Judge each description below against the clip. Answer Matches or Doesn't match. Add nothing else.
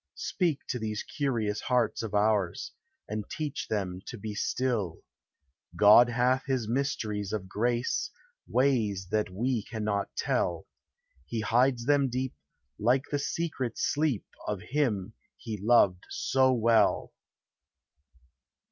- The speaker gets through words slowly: Matches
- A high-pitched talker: Doesn't match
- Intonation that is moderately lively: Matches